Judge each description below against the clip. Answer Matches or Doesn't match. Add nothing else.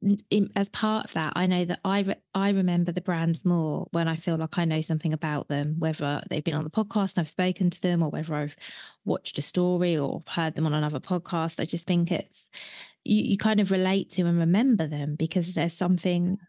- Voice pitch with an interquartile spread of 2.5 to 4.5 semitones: Matches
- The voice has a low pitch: Doesn't match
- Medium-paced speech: Doesn't match